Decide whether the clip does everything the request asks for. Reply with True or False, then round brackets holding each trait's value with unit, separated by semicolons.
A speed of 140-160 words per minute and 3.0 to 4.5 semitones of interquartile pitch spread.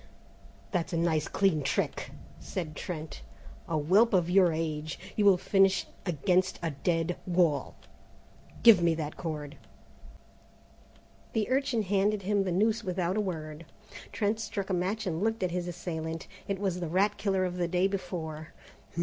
True (155 wpm; 3.3 semitones)